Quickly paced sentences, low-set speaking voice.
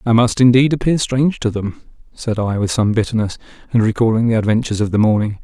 Yes: fast, 210 wpm; low, 115 Hz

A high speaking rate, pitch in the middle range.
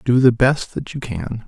No: fast, 245 wpm; low, 120 Hz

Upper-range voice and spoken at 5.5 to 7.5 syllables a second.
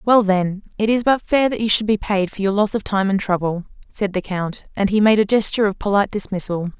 Yes: high, 205 Hz; 5.8 syllables/s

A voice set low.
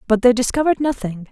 No: high, 245 Hz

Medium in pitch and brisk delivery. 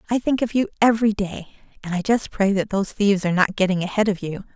No: high, 205 Hz; fast, 250 wpm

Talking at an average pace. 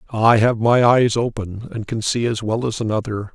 No: fast, 215 wpm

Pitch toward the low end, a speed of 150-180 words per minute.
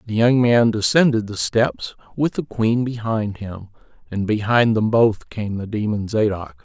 Yes: low, 110 Hz; average, 170 wpm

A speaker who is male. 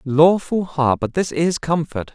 Yes: male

